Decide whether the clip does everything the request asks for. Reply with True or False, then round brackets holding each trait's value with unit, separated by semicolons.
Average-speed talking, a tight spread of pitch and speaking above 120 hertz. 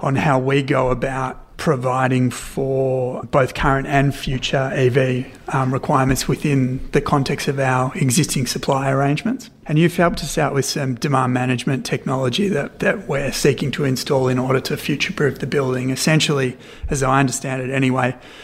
True (165 wpm; 1.9 semitones; 135 Hz)